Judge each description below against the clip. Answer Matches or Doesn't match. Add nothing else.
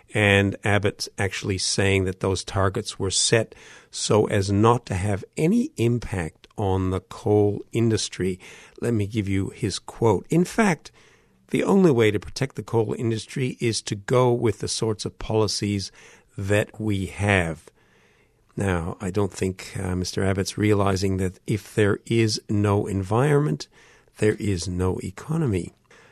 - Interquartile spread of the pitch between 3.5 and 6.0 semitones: Doesn't match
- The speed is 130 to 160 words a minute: Matches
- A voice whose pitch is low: Matches